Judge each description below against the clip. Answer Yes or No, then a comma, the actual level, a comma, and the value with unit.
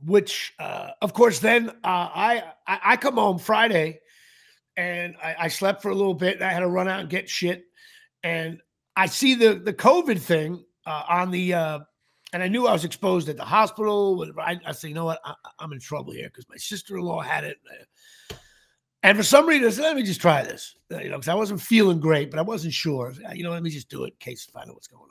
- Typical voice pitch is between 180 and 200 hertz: Yes, medium, 185 Hz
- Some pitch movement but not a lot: Yes, average, 4.6 semitones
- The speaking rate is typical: No, fast, 250 wpm